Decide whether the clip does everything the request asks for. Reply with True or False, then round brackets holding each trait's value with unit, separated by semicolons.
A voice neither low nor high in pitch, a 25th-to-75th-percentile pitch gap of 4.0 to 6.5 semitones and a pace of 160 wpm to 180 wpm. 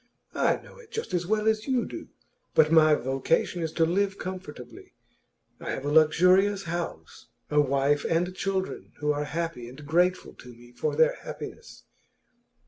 True (165 Hz; 4.5 semitones; 165 wpm)